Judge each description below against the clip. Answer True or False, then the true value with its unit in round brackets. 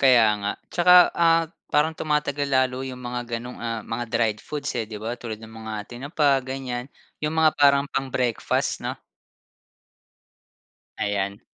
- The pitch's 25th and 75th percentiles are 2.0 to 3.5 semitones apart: False (4.0 semitones)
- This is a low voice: True (125 Hz)